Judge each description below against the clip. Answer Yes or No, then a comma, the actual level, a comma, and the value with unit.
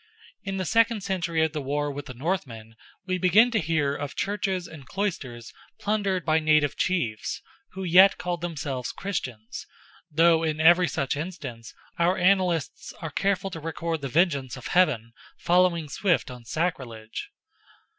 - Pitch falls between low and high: Yes, medium, 165 Hz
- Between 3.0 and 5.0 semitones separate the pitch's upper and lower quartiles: Yes, average, 4.7 semitones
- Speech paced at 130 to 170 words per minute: Yes, average, 155 wpm